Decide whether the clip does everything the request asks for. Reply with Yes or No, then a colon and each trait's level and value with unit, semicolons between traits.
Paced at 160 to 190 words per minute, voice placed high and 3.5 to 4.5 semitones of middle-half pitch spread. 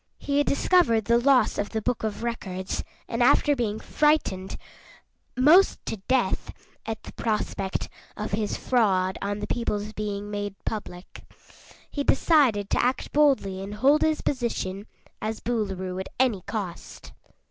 No: average, 145 wpm; high, 220 Hz; average, 4.2 semitones